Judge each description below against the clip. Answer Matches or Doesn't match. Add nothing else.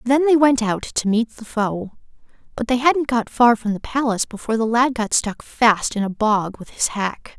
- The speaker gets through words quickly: Matches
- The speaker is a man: Doesn't match